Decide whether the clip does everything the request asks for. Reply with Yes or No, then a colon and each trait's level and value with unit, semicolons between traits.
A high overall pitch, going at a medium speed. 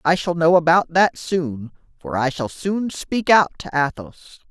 No: medium, 160 Hz; average, 185 wpm